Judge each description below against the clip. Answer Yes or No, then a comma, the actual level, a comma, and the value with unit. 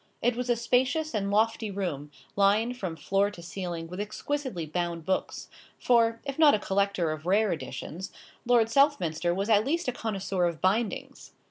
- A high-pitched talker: Yes, high, 200 Hz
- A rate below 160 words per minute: No, average, 170 wpm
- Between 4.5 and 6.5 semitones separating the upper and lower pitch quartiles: Yes, average, 5.0 semitones